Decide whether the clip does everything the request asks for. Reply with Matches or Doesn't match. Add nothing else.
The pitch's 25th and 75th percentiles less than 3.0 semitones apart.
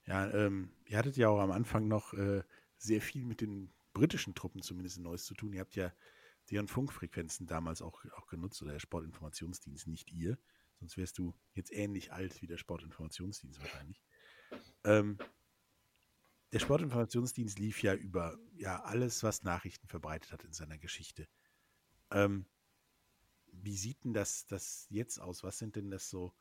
Doesn't match